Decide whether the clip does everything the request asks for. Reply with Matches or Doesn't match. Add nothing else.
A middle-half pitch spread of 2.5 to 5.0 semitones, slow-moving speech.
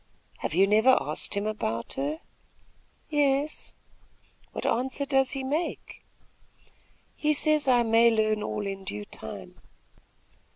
Doesn't match